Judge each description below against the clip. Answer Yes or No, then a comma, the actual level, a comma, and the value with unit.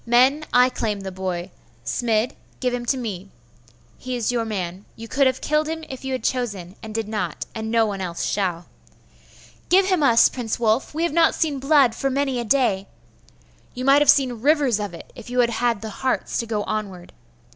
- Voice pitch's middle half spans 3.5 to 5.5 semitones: Yes, average, 4.2 semitones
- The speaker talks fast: Yes, fast, 210 wpm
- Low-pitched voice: No, high, 235 Hz